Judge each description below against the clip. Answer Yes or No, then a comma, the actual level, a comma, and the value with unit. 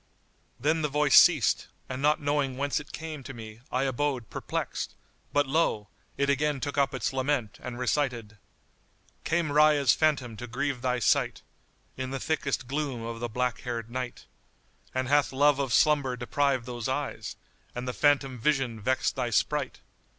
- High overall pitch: No, low, 135 Hz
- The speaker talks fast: No, average, 170 wpm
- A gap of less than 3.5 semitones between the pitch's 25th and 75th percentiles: Yes, average, 2.9 semitones